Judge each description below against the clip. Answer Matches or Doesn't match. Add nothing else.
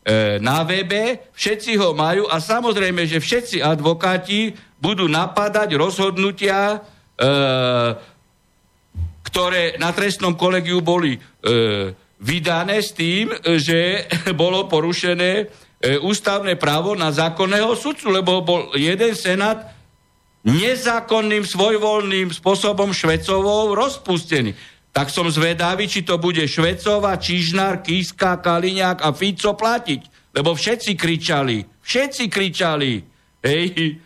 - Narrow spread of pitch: Doesn't match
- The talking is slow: Matches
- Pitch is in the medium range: Matches